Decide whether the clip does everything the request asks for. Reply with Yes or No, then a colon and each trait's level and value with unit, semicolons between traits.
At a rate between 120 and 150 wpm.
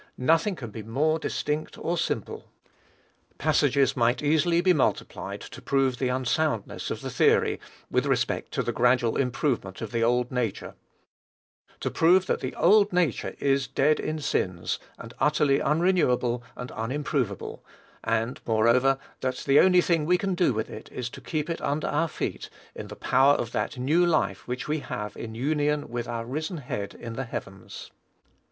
No: average, 170 wpm